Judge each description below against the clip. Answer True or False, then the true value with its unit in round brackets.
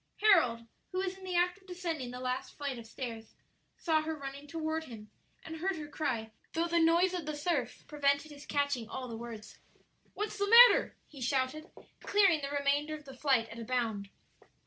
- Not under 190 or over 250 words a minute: True (195 wpm)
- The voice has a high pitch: True (290 Hz)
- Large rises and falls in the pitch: False (5.0 semitones)